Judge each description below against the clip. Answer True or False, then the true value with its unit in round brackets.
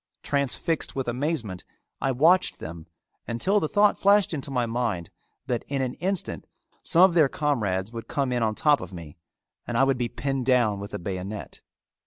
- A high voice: False (125 Hz)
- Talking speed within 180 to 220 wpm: True (185 wpm)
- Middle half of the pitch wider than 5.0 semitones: True (5.5 semitones)